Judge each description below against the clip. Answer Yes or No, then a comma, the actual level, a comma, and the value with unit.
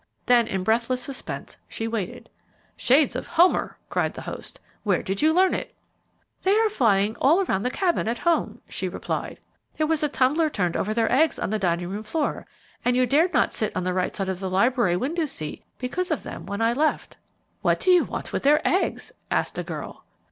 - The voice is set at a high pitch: Yes, very high, 250 Hz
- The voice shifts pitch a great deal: Yes, wide, 7.8 semitones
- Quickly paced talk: Yes, fast, 210 wpm